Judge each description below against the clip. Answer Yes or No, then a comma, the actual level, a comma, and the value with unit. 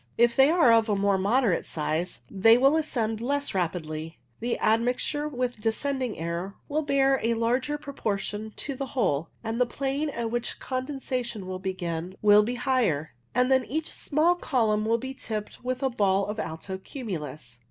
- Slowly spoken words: No, average, 175 wpm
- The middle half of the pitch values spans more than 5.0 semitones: Yes, wide, 5.5 semitones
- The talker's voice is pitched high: Yes, high, 230 Hz